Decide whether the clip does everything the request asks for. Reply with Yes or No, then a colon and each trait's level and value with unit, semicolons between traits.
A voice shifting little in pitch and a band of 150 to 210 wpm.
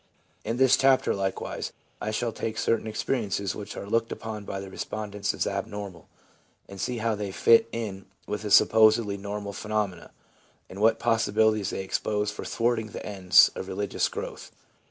Yes: narrow, 2.0 semitones; average, 165 wpm